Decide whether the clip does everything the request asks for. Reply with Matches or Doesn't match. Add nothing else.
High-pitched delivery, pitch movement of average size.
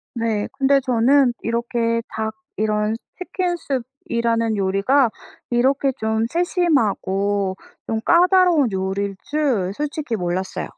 Matches